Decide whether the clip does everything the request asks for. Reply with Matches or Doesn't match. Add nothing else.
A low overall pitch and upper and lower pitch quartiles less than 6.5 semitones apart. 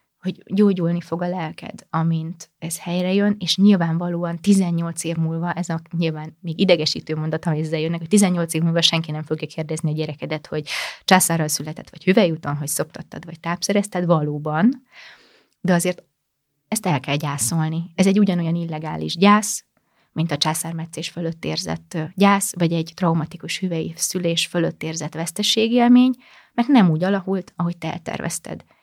Doesn't match